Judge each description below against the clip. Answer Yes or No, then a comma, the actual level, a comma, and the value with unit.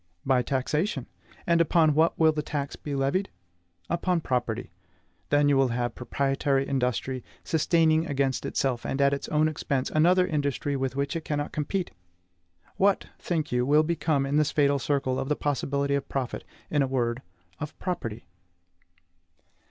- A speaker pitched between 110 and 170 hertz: Yes, medium, 140 Hz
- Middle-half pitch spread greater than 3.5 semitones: No, average, 2.7 semitones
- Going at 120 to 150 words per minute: No, average, 160 wpm